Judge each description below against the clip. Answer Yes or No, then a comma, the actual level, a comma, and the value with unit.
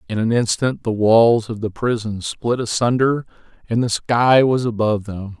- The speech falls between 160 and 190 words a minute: Yes, average, 180 wpm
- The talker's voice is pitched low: Yes, low, 115 Hz